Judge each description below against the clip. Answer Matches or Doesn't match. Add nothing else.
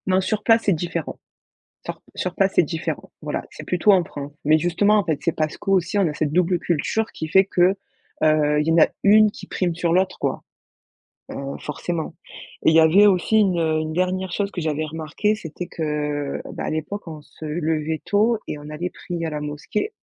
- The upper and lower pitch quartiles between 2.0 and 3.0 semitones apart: Doesn't match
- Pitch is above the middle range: Doesn't match